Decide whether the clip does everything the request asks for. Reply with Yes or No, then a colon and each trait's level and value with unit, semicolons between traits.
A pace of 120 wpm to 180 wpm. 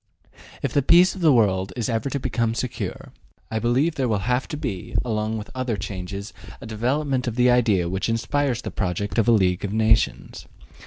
No: average, 200 wpm